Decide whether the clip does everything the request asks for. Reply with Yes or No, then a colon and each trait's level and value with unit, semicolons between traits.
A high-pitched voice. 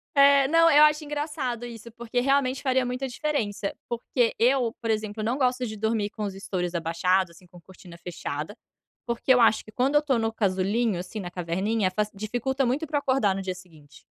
Yes: high, 225 Hz